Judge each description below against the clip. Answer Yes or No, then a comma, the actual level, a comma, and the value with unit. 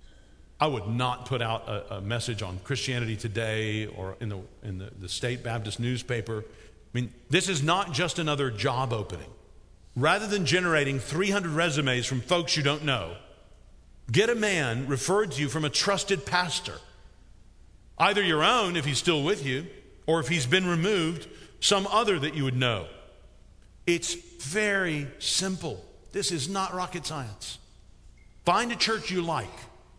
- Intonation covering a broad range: Yes, wide, 7.7 semitones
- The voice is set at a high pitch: No, medium, 140 Hz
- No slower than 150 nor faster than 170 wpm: Yes, average, 160 wpm